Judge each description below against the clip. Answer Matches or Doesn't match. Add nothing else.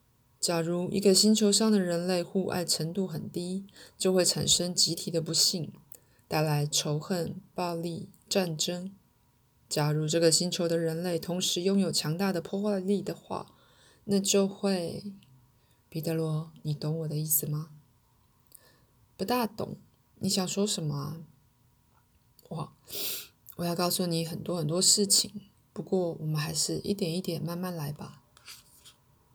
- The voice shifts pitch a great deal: Doesn't match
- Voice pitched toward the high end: Doesn't match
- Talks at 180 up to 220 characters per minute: Matches